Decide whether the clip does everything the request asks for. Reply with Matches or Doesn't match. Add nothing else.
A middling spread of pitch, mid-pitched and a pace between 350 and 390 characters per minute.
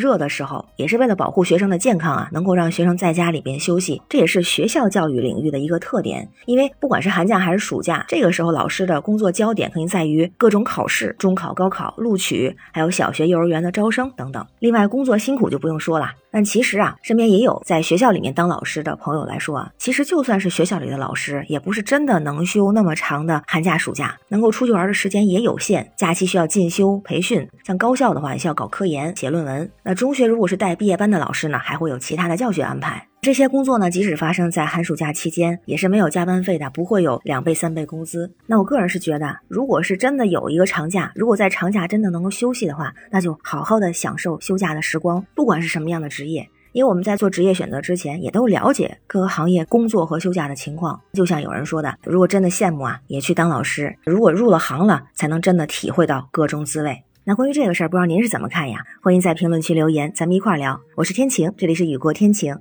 Matches